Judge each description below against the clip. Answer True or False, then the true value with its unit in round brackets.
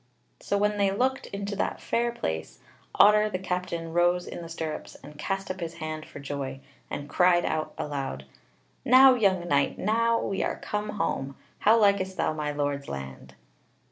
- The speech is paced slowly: False (175 wpm)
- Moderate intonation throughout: False (5.7 semitones)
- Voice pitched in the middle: True (175 Hz)